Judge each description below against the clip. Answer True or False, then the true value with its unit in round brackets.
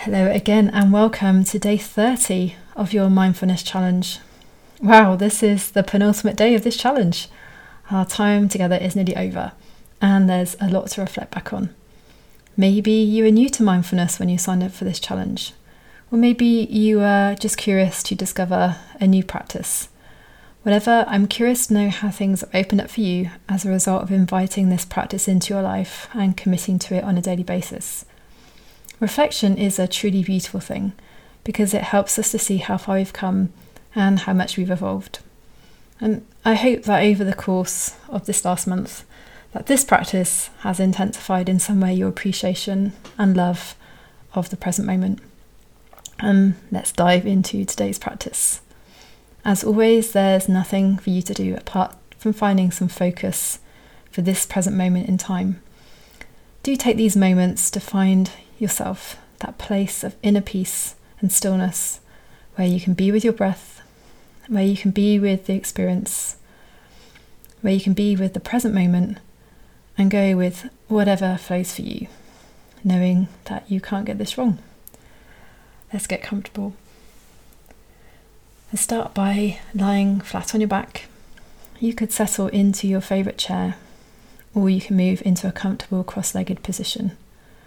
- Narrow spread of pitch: True (1.8 semitones)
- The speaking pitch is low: False (195 Hz)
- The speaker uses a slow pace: False (165 wpm)